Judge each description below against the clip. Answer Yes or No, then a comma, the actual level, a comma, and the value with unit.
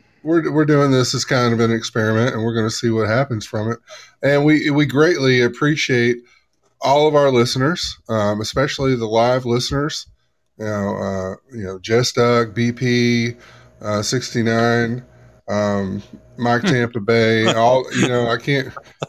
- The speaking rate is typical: Yes, average, 165 wpm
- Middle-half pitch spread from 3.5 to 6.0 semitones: No, narrow, 2.5 semitones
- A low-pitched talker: Yes, low, 120 Hz